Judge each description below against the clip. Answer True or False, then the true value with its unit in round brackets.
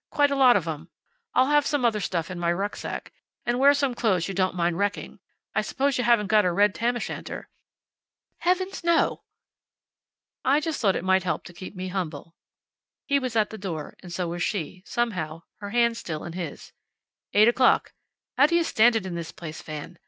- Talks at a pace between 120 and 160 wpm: False (205 wpm)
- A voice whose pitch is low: False (205 Hz)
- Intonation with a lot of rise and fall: True (6.0 semitones)